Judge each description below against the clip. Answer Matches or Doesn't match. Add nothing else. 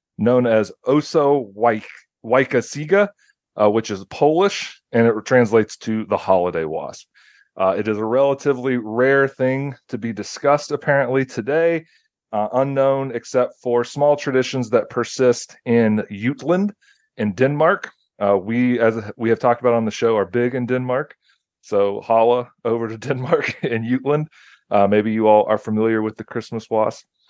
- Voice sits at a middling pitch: Doesn't match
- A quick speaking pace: Doesn't match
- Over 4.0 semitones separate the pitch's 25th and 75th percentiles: Doesn't match